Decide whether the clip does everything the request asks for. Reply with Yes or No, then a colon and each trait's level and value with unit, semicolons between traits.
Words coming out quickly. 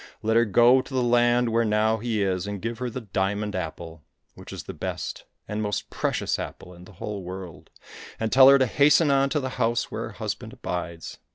Yes: fast, 215 wpm